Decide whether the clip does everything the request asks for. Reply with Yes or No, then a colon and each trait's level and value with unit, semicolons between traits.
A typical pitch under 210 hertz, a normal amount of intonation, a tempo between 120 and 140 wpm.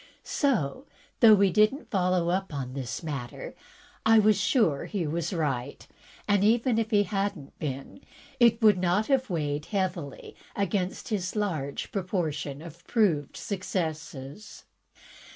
No: medium, 185 Hz; wide, 5.7 semitones; slow, 135 wpm